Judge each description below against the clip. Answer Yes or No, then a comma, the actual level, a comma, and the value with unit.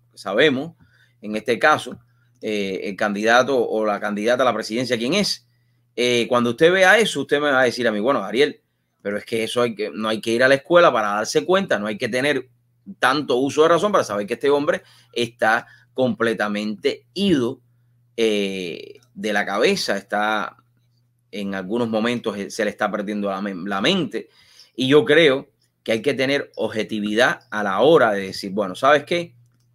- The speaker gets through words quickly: No, average, 185 wpm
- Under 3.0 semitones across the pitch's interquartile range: No, average, 4.2 semitones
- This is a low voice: Yes, low, 120 Hz